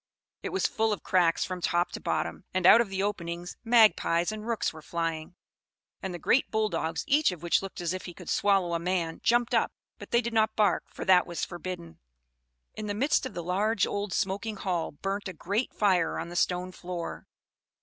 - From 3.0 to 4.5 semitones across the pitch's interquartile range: Yes, average, 3.7 semitones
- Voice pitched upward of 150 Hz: Yes, medium, 185 Hz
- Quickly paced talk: Yes, fast, 210 wpm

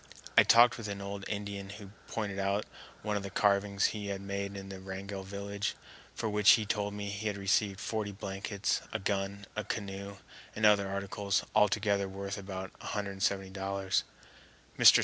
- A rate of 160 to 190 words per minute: Yes, average, 170 wpm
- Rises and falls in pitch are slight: Yes, narrow, 0.9 semitones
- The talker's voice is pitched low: Yes, low, 100 Hz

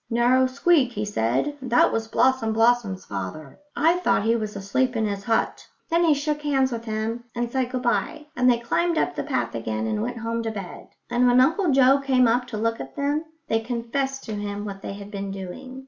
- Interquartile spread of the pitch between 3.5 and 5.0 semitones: Yes, average, 4.2 semitones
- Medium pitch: No, high, 235 Hz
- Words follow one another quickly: Yes, fast, 220 wpm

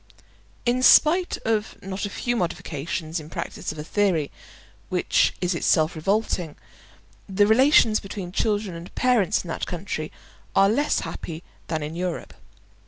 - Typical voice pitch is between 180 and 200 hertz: Yes, high, 190 Hz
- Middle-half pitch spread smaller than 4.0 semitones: No, average, 4.8 semitones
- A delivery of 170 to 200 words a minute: No, average, 145 wpm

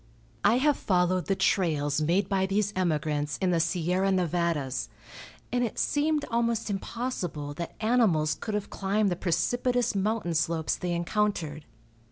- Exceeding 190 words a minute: No, average, 145 wpm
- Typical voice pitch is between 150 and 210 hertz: Yes, medium, 185 Hz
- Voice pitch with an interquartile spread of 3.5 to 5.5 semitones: Yes, average, 4.5 semitones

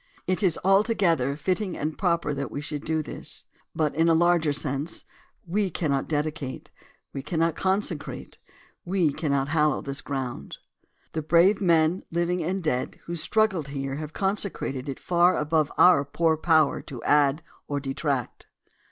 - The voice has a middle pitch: Yes, medium, 160 Hz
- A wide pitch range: No, average, 3.5 semitones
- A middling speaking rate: Yes, average, 160 wpm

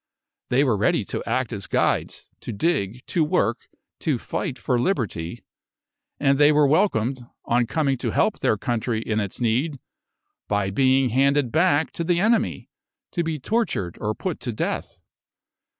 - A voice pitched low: Yes, low, 130 Hz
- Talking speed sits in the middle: Yes, average, 160 wpm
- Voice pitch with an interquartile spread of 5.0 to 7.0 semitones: Yes, wide, 5.6 semitones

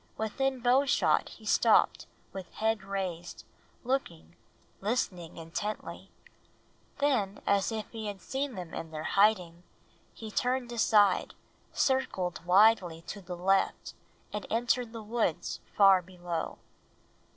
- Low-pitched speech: No, high, 205 Hz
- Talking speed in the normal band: No, slow, 120 wpm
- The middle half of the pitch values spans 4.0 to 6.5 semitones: Yes, average, 4.7 semitones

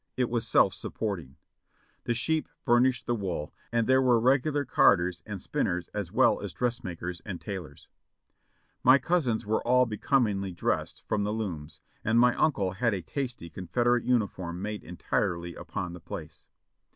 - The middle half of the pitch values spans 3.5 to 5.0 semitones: No, wide, 5.5 semitones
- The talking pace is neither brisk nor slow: Yes, average, 155 wpm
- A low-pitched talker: Yes, low, 105 Hz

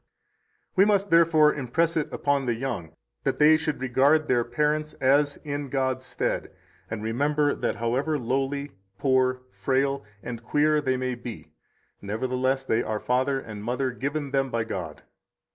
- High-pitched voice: No, low, 135 Hz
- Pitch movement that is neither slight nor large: Yes, average, 3.1 semitones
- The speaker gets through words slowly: No, average, 160 wpm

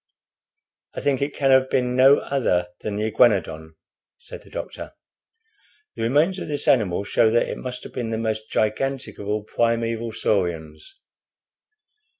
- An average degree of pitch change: Yes, average, 4.1 semitones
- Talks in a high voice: No, low, 115 Hz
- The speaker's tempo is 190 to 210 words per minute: No, average, 160 wpm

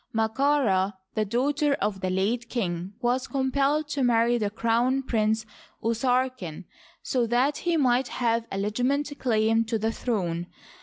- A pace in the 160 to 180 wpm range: No, average, 145 wpm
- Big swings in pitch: No, average, 3.6 semitones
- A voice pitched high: Yes, high, 235 Hz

